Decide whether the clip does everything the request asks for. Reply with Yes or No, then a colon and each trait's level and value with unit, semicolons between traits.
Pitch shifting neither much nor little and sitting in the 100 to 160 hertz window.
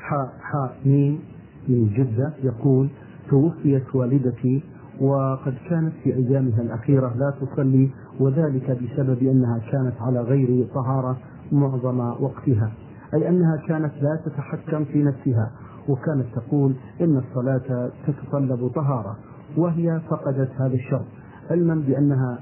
No: narrow, 2.3 semitones; low, 135 Hz